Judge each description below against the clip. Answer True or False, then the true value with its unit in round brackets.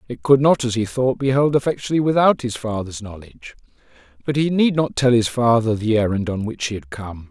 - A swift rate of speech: True (220 wpm)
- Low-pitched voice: True (120 Hz)